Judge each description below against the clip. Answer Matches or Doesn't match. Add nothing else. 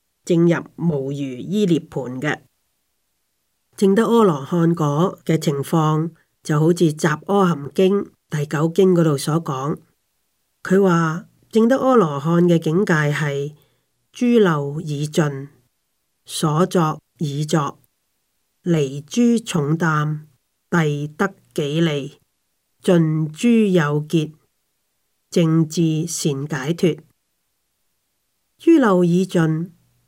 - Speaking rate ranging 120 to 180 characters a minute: Matches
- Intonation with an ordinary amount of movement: Matches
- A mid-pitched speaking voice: Matches